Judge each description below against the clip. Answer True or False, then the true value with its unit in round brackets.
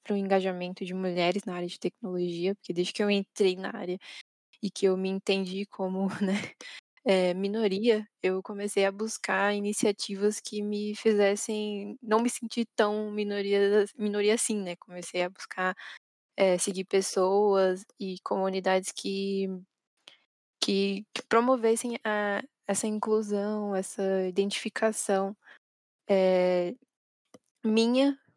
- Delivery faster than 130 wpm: False (125 wpm)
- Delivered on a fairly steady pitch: True (2.0 semitones)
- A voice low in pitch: False (200 Hz)